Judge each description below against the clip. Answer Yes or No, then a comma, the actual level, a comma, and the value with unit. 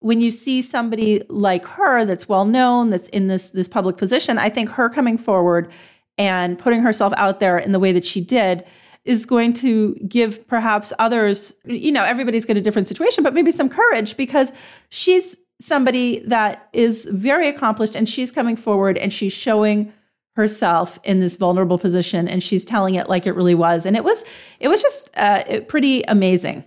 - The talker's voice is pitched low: No, high, 215 Hz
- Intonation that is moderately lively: Yes, average, 4.3 semitones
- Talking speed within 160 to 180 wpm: No, average, 190 wpm